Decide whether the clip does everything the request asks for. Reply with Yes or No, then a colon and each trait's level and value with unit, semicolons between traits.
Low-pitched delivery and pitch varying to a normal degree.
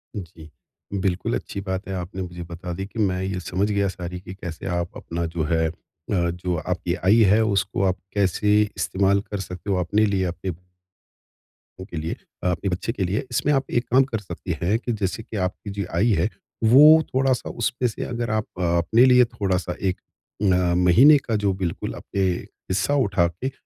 Yes: very low, 95 Hz; average, 3.1 semitones